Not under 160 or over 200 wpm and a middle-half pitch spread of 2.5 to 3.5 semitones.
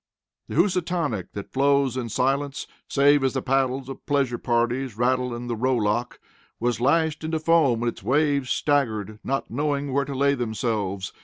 Yes: average, 170 wpm; average, 3.1 semitones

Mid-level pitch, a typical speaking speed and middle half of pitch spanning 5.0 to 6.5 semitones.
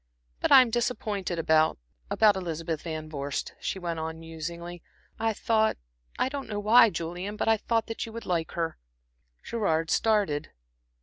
Yes: medium, 180 Hz; average, 160 wpm; wide, 5.4 semitones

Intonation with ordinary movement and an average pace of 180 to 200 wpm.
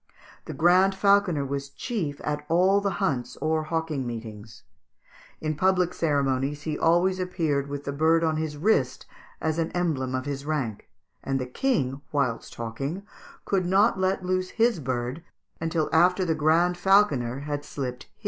No: average, 4.7 semitones; average, 160 wpm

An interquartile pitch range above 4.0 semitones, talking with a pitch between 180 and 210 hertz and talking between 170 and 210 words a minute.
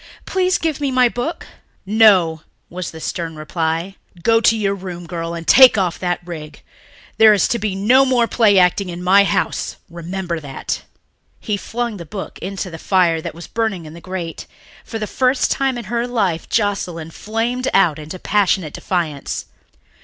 Yes: average, 4.9 semitones; high, 190 Hz; average, 175 wpm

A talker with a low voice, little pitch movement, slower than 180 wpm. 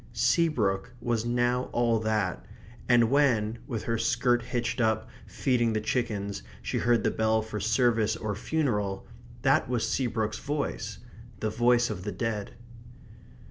Yes: low, 115 Hz; narrow, 2.1 semitones; average, 140 wpm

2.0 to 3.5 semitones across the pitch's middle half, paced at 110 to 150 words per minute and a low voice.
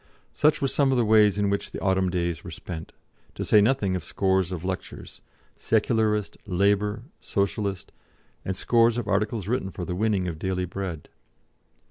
No: average, 2.9 semitones; average, 170 wpm; low, 100 Hz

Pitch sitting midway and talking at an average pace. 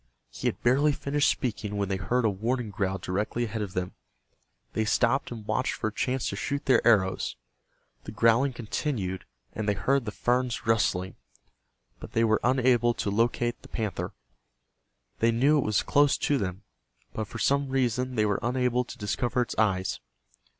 No: low, 115 Hz; average, 180 wpm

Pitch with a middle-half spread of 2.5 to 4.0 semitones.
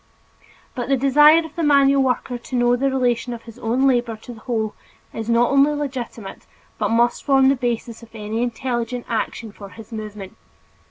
Yes: average, 2.9 semitones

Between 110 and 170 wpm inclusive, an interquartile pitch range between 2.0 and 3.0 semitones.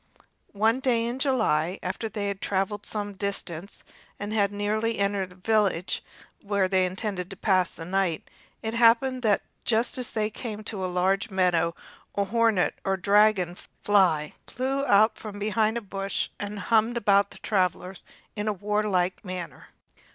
Yes: average, 160 wpm; narrow, 2.6 semitones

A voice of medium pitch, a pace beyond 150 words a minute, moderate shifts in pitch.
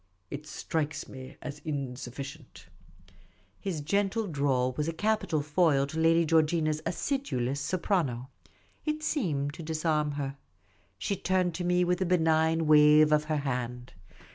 No: medium, 155 Hz; average, 140 wpm; average, 3.5 semitones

